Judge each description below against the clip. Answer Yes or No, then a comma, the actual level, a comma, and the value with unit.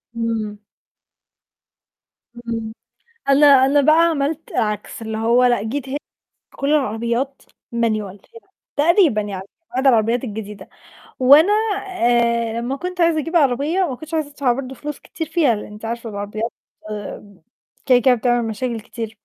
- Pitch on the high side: Yes, high, 245 Hz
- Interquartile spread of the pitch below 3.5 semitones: No, average, 4.3 semitones